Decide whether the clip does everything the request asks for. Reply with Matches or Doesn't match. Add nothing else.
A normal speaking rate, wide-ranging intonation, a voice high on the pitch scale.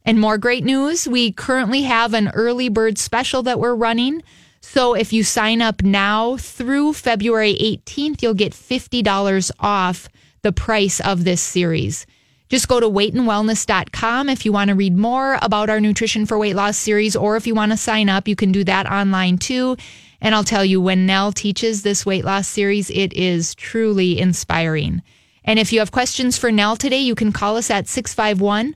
Doesn't match